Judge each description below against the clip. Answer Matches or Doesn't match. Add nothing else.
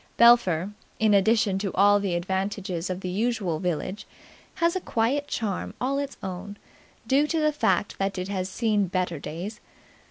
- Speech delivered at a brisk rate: Doesn't match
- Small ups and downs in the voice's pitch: Doesn't match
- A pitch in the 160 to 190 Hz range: Doesn't match